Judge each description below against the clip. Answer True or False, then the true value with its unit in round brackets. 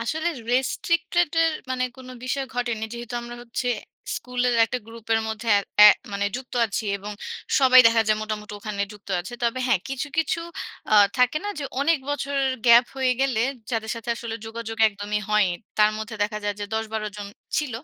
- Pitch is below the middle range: False (235 Hz)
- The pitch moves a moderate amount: True (3.3 semitones)